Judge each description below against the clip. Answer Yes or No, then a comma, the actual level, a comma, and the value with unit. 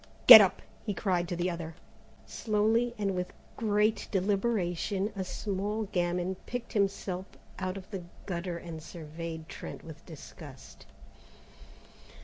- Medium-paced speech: No, slow, 130 wpm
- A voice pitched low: No, medium, 185 Hz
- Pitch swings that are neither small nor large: Yes, average, 3.2 semitones